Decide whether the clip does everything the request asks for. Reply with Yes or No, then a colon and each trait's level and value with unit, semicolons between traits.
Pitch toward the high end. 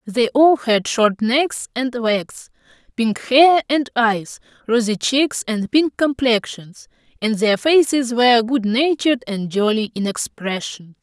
Yes: high, 240 Hz